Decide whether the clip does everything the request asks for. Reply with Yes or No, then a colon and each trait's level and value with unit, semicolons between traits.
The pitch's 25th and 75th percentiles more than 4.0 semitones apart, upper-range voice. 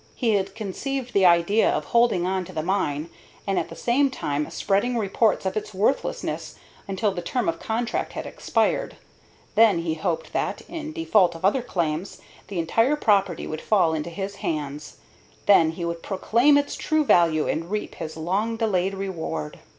Yes: average, 5.1 semitones; high, 195 Hz